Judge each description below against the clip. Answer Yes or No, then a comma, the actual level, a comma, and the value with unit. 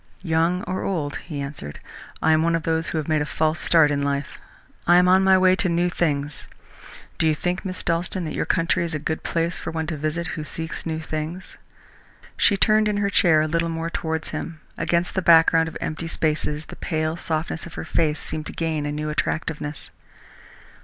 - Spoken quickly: Yes, fast, 215 wpm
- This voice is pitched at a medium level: Yes, medium, 160 Hz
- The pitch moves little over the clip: Yes, narrow, 1.8 semitones